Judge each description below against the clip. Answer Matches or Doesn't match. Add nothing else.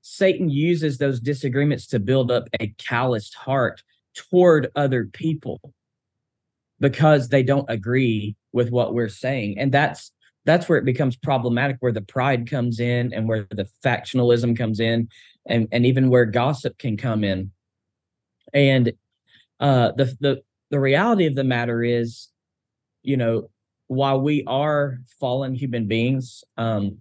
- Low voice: Matches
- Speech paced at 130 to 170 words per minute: Matches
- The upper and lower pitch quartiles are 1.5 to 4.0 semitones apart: Matches